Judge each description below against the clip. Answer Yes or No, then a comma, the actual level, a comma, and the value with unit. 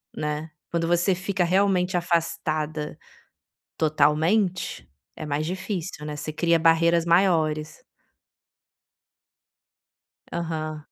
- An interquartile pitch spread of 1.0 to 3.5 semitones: Yes, narrow, 2.5 semitones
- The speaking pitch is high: No, medium, 165 Hz